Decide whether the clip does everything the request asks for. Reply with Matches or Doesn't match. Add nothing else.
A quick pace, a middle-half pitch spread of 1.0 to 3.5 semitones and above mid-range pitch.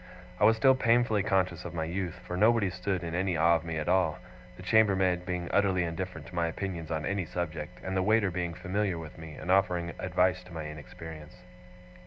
Doesn't match